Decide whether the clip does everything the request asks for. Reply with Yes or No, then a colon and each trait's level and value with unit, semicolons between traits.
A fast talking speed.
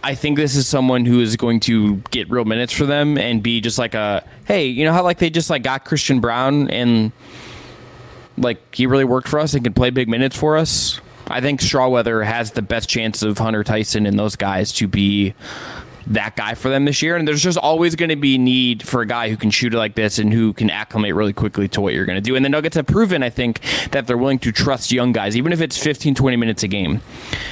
Yes: fast, 255 wpm